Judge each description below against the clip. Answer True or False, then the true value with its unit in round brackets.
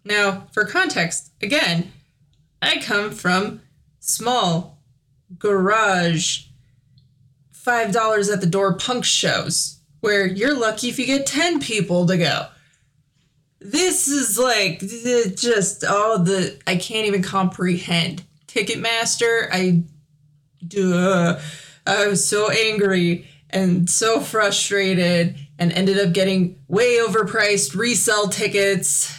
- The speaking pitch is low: False (190 Hz)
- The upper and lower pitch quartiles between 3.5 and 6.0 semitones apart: True (5.0 semitones)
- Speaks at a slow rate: True (110 wpm)